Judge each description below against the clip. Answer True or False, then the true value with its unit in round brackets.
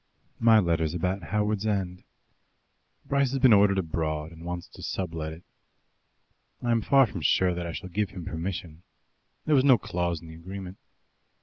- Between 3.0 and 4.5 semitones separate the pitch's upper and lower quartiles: True (4.1 semitones)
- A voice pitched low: True (90 Hz)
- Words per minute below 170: False (175 wpm)